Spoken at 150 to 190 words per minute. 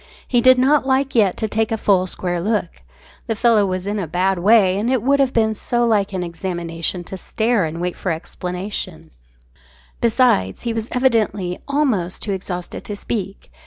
Yes: average, 185 wpm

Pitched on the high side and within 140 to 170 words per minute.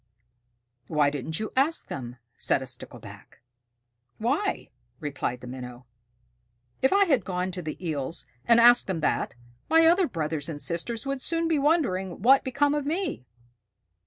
Yes: high, 195 Hz; average, 160 wpm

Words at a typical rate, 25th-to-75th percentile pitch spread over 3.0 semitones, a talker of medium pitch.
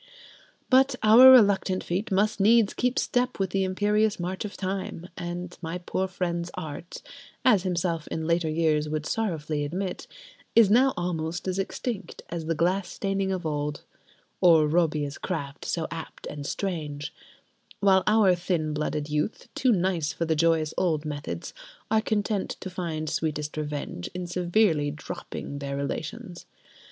Yes: average, 150 wpm; average, 4.1 semitones; medium, 175 Hz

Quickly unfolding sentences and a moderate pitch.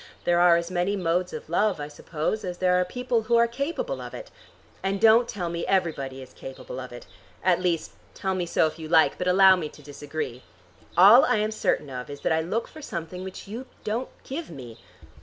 Yes: fast, 220 wpm; medium, 180 Hz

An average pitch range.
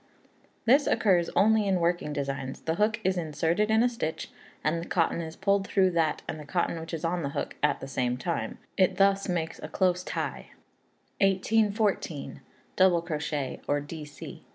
Yes: average, 4.2 semitones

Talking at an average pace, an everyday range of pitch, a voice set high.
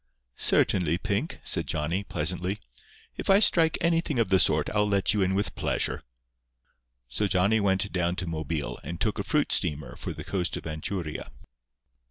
No: average, 170 wpm; average, 3.8 semitones; very low, 95 Hz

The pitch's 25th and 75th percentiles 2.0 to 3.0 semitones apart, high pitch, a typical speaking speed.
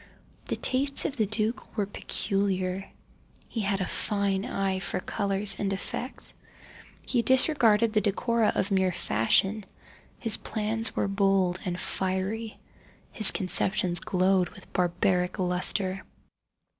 No: narrow, 2.6 semitones; high, 195 Hz; slow, 130 wpm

